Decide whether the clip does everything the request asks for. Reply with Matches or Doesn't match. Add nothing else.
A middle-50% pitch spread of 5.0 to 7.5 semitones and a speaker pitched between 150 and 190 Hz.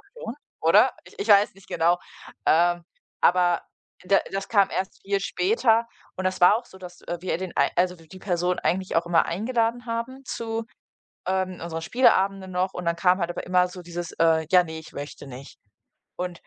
Doesn't match